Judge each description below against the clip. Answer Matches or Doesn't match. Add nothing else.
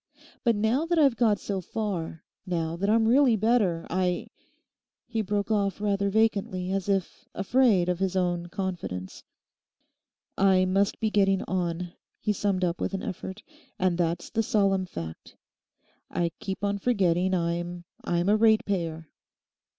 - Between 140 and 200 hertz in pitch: Matches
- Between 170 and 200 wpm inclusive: Doesn't match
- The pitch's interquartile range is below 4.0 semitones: Matches